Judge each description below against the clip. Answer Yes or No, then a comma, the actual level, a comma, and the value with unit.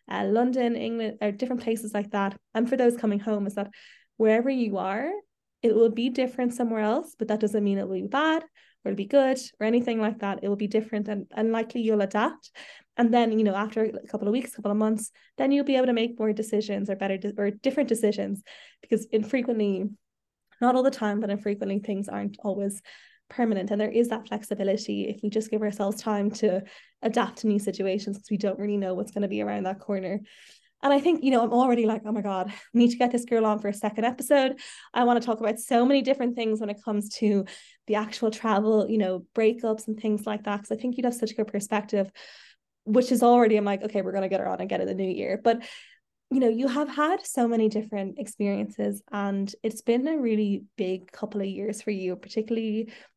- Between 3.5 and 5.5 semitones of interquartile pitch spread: No, average, 2.8 semitones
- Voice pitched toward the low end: No, high, 215 Hz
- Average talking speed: No, fast, 235 wpm